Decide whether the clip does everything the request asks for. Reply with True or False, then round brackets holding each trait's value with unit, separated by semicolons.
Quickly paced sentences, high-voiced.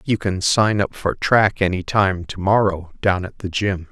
False (215 wpm; 95 Hz)